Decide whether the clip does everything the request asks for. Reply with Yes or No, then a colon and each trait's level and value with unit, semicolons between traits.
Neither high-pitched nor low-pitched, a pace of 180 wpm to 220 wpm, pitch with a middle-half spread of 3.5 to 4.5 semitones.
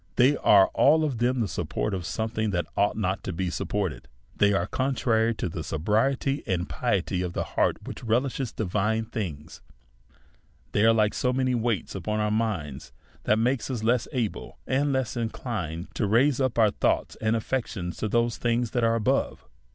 No: low, 110 Hz; average, 185 wpm; average, 4.0 semitones